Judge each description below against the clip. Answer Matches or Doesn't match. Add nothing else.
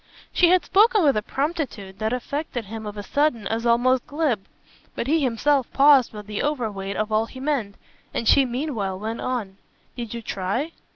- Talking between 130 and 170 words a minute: Doesn't match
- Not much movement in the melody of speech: Doesn't match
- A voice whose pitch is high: Matches